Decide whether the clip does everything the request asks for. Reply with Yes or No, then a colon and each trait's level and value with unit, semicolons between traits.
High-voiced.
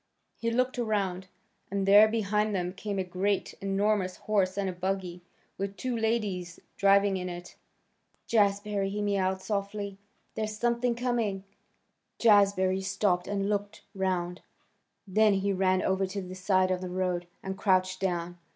Yes: high, 195 Hz